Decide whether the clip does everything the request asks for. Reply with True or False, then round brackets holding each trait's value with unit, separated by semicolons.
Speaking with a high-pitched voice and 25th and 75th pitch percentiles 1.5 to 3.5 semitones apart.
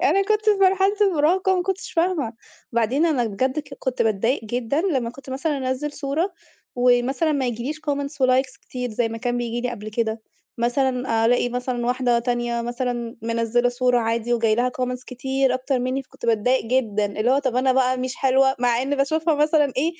True (255 Hz; 2.9 semitones)